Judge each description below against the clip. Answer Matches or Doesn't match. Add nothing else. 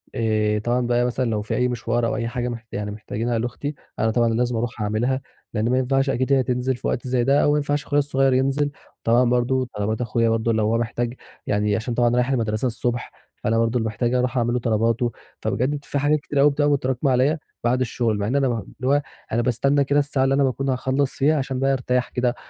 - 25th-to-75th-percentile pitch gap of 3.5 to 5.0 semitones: Doesn't match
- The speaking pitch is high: Doesn't match